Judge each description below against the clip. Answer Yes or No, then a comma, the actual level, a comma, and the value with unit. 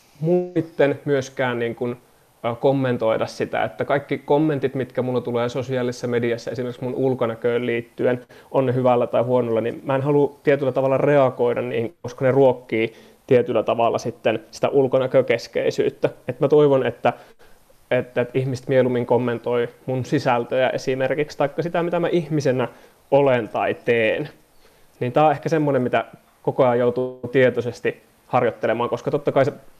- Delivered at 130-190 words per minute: Yes, average, 145 wpm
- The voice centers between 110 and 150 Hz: Yes, low, 130 Hz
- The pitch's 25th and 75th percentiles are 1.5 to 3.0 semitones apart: Yes, average, 2.7 semitones